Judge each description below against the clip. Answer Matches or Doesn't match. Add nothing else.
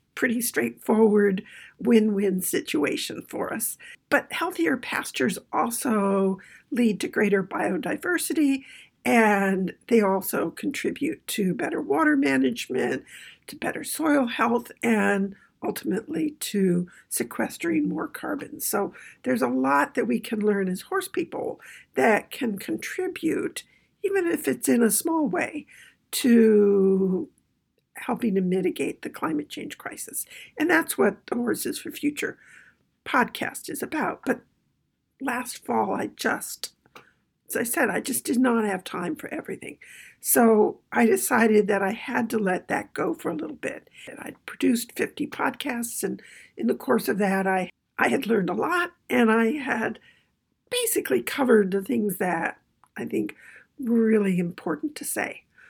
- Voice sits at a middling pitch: Doesn't match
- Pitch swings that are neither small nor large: Doesn't match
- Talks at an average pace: Matches